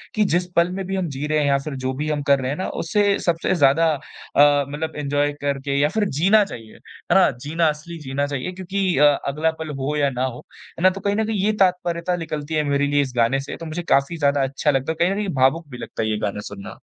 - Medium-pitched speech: Yes, medium, 150 Hz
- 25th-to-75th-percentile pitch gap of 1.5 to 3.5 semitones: No, average, 4.1 semitones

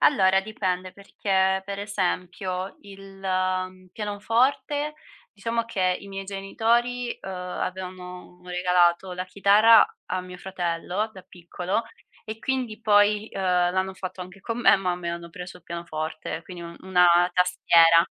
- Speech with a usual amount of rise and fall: No, narrow, 2.3 semitones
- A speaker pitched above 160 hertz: Yes, high, 190 Hz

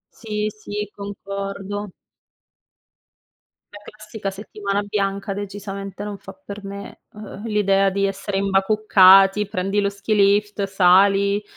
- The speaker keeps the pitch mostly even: Yes, narrow, 1.0 semitones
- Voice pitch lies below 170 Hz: No, high, 200 Hz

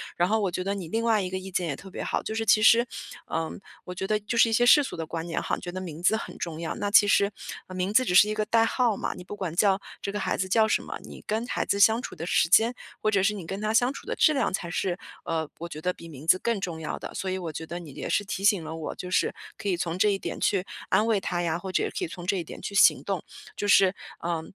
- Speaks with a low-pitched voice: No, high, 190 Hz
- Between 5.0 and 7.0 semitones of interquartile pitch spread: No, average, 3.7 semitones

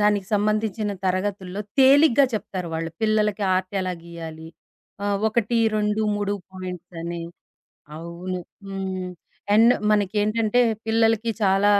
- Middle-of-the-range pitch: No, high, 205 Hz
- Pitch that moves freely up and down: No, average, 2.7 semitones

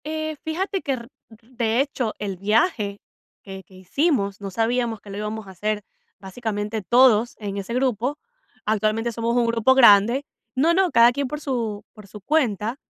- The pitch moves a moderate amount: Yes, average, 3.8 semitones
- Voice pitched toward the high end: Yes, high, 230 Hz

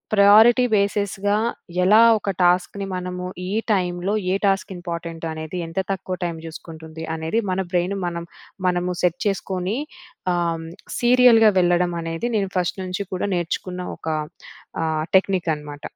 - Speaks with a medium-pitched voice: Yes, medium, 180 Hz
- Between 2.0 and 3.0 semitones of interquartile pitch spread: Yes, average, 2.7 semitones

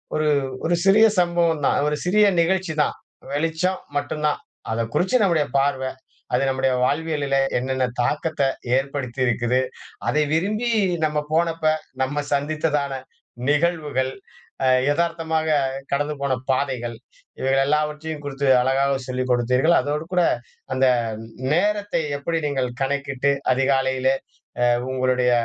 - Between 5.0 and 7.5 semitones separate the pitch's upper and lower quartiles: No, average, 3.5 semitones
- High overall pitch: No, medium, 145 Hz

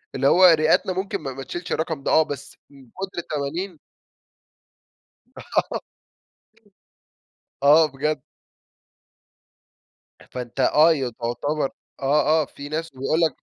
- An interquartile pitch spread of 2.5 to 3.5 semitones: Yes, average, 3.0 semitones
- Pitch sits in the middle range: Yes, medium, 150 Hz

